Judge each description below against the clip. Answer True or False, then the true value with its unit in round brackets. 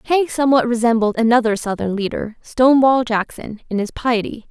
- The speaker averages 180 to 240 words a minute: False (145 wpm)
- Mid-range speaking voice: False (235 Hz)